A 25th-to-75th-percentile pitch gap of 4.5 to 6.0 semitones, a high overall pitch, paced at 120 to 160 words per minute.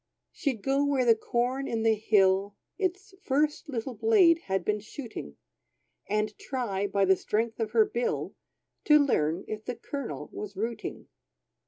Yes: average, 4.8 semitones; high, 230 Hz; average, 155 wpm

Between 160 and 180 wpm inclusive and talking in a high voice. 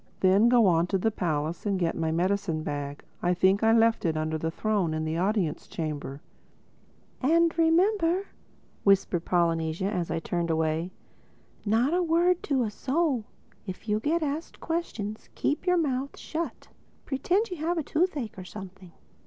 Yes: average, 165 wpm; high, 205 Hz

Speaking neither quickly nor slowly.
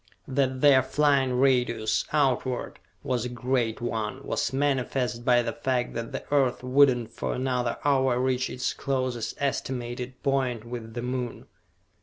Yes: average, 150 wpm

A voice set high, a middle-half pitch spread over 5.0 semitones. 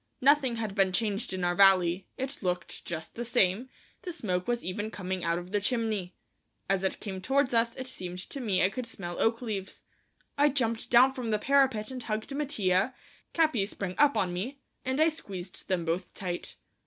Yes: high, 215 Hz; wide, 5.5 semitones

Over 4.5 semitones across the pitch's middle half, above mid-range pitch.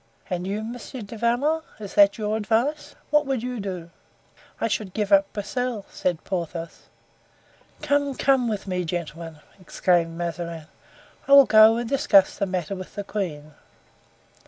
Yes: average, 5.1 semitones; high, 205 Hz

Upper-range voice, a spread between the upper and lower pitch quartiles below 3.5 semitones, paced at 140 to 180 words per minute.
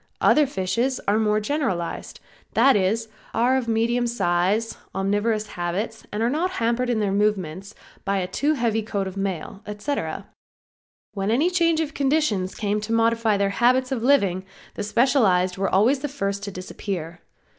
No: high, 215 Hz; average, 4.3 semitones; average, 160 wpm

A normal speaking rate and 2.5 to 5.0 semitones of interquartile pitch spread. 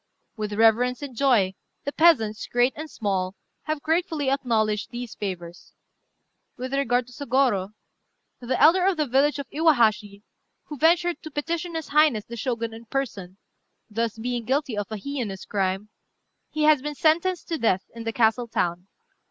No: average, 160 wpm; wide, 5.6 semitones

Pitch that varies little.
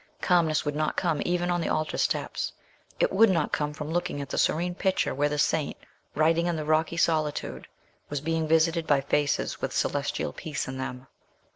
Yes: narrow, 2.3 semitones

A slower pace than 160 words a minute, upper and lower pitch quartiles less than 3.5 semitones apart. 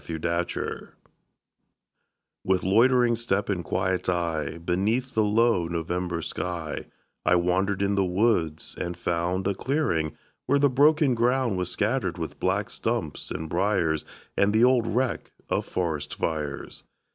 No: average, 140 wpm; wide, 5.4 semitones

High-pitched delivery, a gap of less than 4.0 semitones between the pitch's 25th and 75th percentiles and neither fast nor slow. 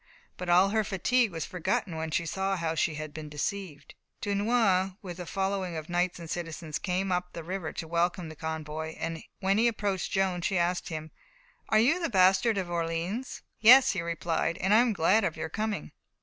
No: medium, 180 Hz; average, 3.2 semitones; average, 195 wpm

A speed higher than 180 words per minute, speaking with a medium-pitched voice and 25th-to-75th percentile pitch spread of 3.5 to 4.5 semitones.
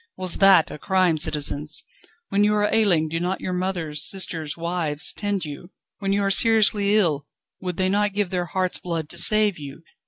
Yes: average, 190 wpm; medium, 180 Hz; average, 3.8 semitones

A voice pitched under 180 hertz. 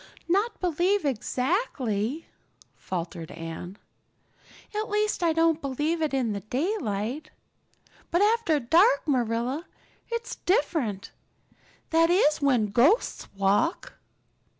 No: very high, 300 Hz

